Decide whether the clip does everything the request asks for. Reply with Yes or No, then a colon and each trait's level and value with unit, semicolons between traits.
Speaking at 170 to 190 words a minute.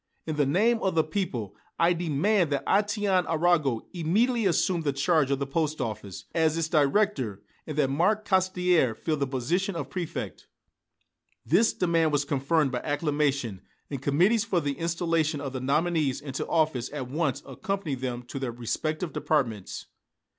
No: average, 160 wpm